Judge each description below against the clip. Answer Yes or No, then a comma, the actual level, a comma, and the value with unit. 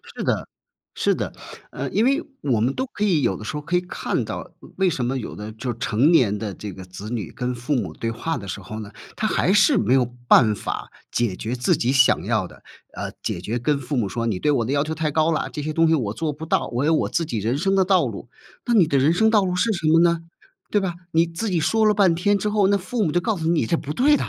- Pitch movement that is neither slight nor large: No, wide, 7.1 semitones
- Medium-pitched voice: Yes, medium, 150 Hz